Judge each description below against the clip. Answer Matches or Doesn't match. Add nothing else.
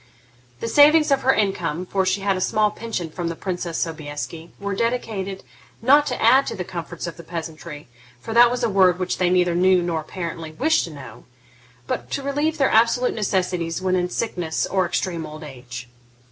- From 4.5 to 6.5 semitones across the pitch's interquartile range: Matches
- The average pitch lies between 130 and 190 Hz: Matches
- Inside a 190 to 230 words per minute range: Matches